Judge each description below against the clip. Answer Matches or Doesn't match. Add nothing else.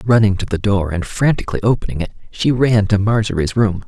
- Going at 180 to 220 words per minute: Matches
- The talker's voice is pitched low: Matches